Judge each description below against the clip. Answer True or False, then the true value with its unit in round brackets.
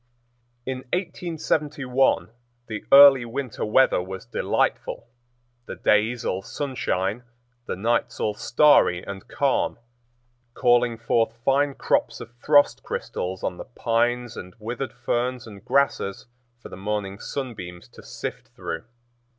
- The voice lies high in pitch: False (120 Hz)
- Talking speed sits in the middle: False (125 wpm)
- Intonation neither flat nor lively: True (4.5 semitones)